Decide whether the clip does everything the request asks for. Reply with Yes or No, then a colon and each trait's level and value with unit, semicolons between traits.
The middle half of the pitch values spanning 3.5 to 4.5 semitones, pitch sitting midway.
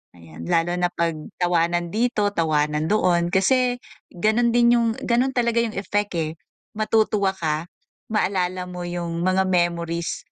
Yes: average, 4.2 semitones; medium, 180 Hz